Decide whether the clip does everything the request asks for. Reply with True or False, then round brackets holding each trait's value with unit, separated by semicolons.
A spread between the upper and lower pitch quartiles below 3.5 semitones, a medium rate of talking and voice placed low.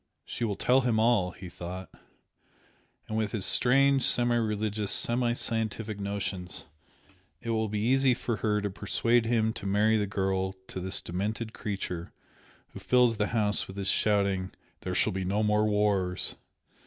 True (2.9 semitones; 165 wpm; 105 Hz)